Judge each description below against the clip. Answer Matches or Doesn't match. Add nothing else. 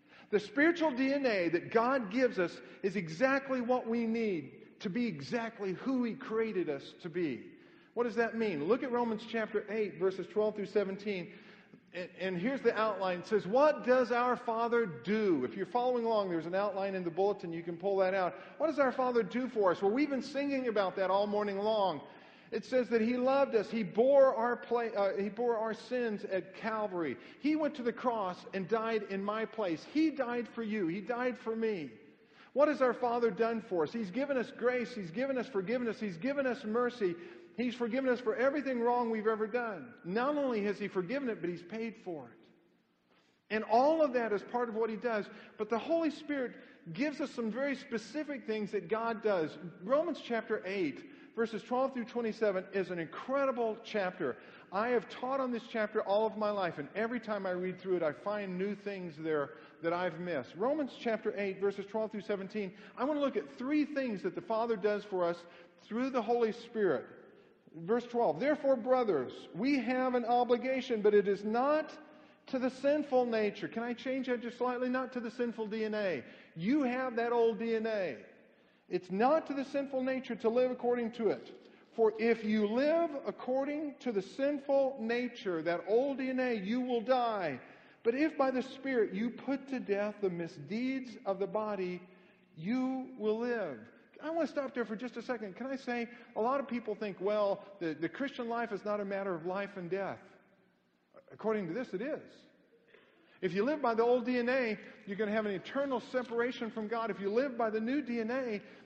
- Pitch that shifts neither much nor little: Matches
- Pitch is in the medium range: Doesn't match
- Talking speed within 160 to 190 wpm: Doesn't match